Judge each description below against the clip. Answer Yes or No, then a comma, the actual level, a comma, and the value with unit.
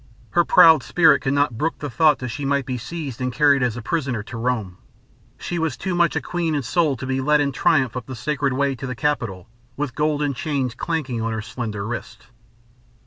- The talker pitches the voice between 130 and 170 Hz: Yes, low, 135 Hz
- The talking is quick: Yes, fast, 220 wpm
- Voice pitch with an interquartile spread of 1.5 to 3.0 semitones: No, average, 3.7 semitones